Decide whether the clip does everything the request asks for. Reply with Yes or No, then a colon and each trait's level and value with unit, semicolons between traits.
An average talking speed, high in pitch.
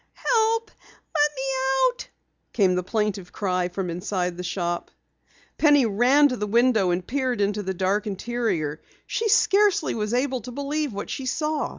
Yes: average, 165 wpm; high, 220 Hz